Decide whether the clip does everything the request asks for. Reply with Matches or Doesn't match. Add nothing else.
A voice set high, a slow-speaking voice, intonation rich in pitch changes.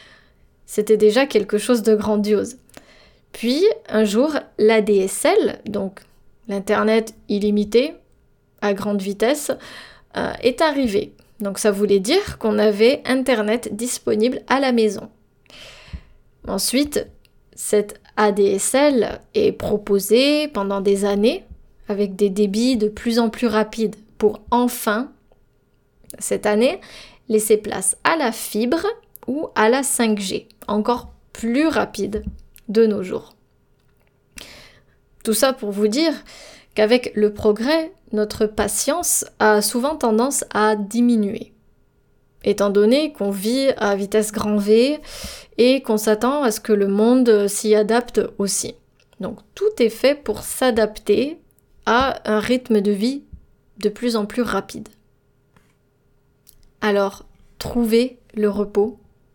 Doesn't match